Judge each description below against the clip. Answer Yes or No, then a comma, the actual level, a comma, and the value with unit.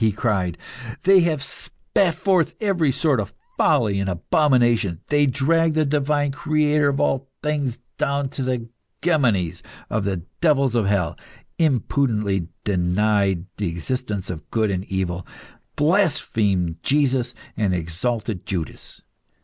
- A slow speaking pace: Yes, slow, 125 wpm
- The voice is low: Yes, low, 125 Hz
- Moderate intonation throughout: No, wide, 7.2 semitones